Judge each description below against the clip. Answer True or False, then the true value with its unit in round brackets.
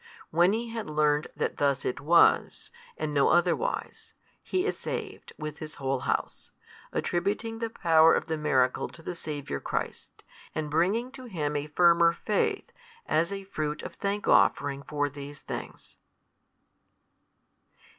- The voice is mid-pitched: True (160 Hz)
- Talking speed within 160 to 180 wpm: False (145 wpm)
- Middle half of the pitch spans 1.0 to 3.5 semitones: False (5.2 semitones)